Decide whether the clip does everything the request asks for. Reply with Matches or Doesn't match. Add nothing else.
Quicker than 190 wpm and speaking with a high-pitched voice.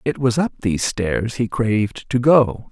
Doesn't match